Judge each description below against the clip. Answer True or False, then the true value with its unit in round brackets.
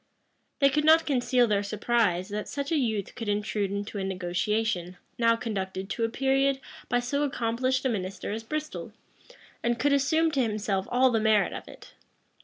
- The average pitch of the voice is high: True (230 Hz)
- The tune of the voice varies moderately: True (4.7 semitones)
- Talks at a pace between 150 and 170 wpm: False (185 wpm)